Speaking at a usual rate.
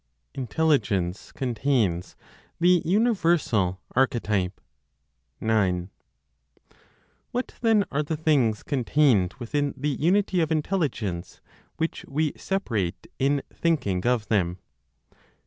No: slow, 95 wpm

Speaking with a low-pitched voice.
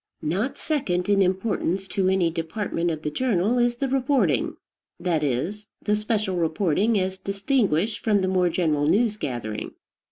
No: high, 190 Hz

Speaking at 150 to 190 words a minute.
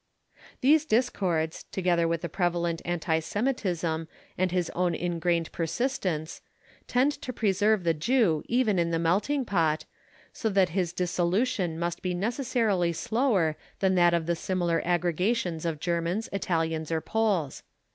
No: average, 140 wpm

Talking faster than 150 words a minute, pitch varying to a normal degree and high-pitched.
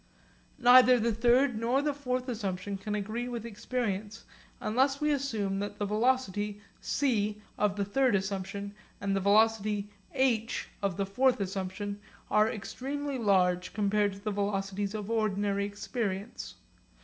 No: average, 140 wpm; average, 3.6 semitones; high, 210 Hz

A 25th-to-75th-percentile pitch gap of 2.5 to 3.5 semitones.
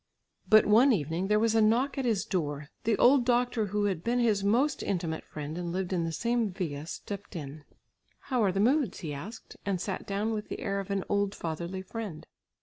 No: average, 4.7 semitones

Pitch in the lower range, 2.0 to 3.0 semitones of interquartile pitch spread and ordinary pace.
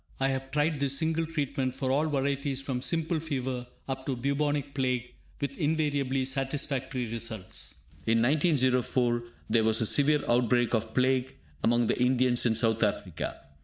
Yes: low, 130 Hz; average, 2.7 semitones; average, 155 wpm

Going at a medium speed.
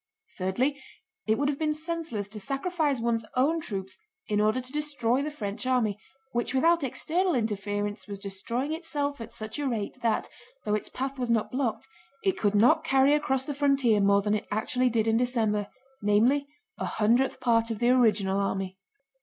Yes: average, 180 wpm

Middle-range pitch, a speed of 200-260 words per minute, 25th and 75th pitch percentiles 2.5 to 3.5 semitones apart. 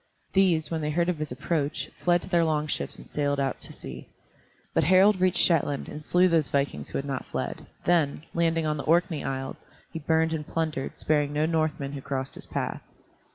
Yes: medium, 155 Hz; fast, 205 wpm; average, 2.8 semitones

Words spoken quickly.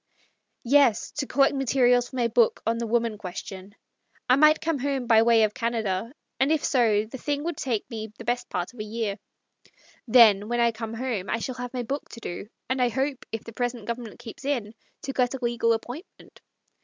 Yes: fast, 220 wpm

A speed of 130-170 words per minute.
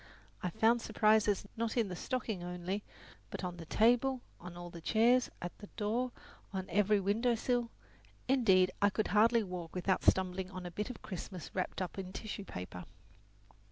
No: average, 180 wpm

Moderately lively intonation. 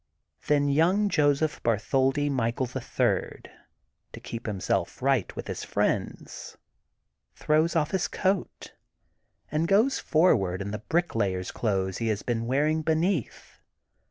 No: wide, 6.0 semitones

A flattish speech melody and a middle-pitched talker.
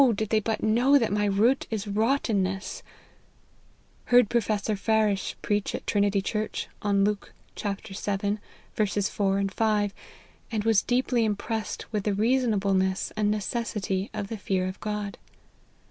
No: narrow, 1.8 semitones; high, 210 Hz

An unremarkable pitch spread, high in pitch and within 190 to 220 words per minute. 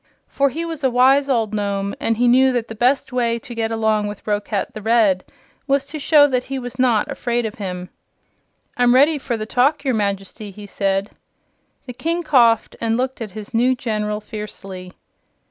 Yes: average, 3.7 semitones; high, 230 Hz; average, 195 wpm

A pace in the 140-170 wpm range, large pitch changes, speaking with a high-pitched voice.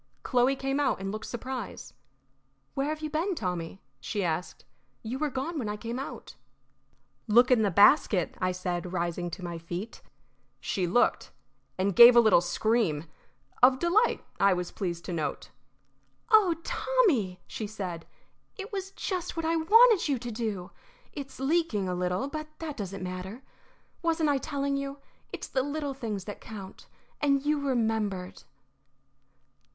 Yes: average, 155 wpm; wide, 7.7 semitones; high, 235 Hz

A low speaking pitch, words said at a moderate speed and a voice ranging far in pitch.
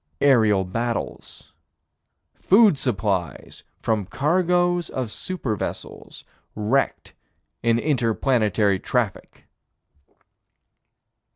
No: low, 120 Hz; slow, 75 wpm; wide, 5.7 semitones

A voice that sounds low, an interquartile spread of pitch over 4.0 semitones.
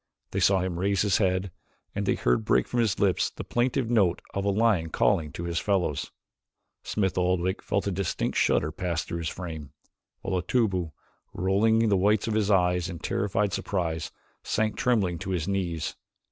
No: very low, 95 Hz; average, 3.0 semitones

